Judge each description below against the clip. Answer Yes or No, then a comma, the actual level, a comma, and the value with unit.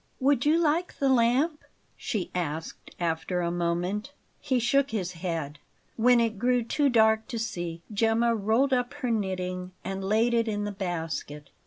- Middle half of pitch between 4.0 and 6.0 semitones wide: Yes, wide, 5.5 semitones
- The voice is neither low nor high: No, high, 220 Hz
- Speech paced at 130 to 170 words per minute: Yes, average, 165 wpm